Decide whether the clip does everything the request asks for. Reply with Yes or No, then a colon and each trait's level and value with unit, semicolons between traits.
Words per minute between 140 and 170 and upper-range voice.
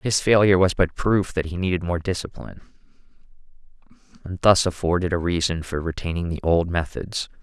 No: average, 160 wpm; very low, 90 Hz